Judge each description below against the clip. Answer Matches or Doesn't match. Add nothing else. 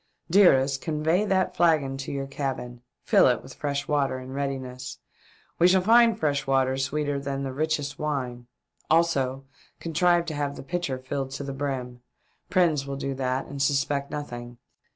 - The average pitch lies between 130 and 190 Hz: Matches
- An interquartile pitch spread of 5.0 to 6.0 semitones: Doesn't match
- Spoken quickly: Doesn't match